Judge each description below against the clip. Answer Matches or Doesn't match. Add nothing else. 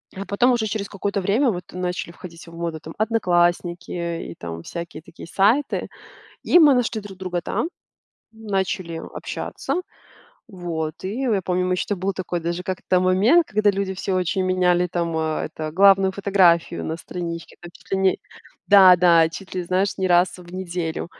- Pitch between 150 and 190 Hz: Matches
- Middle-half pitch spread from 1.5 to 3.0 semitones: Matches